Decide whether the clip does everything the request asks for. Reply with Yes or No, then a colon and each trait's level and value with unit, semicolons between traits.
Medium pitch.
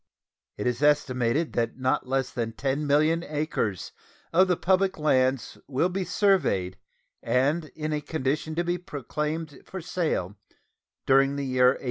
Yes: medium, 145 Hz